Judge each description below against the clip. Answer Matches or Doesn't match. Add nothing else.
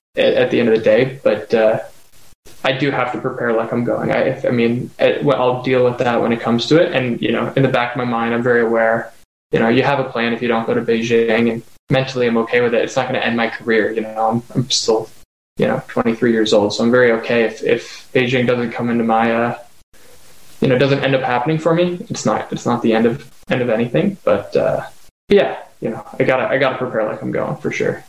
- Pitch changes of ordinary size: Doesn't match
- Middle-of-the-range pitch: Doesn't match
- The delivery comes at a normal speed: Doesn't match